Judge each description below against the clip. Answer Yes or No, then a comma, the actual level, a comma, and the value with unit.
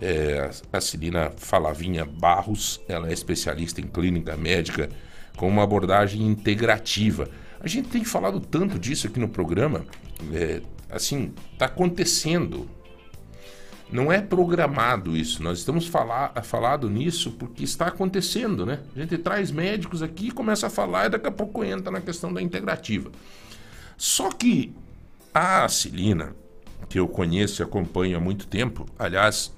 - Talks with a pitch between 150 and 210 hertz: No, low, 100 Hz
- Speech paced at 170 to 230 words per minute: No, average, 145 wpm